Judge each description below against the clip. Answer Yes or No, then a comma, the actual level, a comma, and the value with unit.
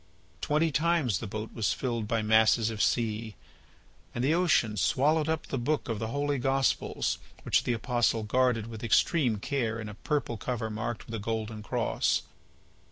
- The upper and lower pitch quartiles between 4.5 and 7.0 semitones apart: No, average, 3.8 semitones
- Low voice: Yes, low, 115 Hz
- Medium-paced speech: Yes, average, 170 wpm